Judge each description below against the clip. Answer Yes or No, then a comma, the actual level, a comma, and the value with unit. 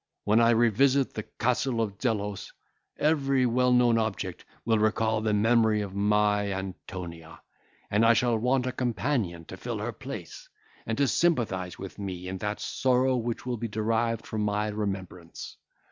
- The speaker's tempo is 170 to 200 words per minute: No, average, 160 wpm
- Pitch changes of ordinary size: Yes, average, 3.2 semitones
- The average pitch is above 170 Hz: No, low, 110 Hz